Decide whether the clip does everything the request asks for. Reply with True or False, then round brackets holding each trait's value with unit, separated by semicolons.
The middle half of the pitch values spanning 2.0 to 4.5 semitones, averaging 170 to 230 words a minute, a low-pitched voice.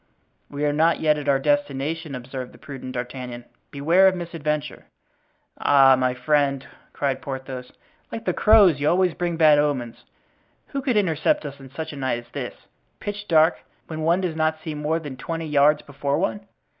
False (3.3 semitones; 180 wpm; 150 Hz)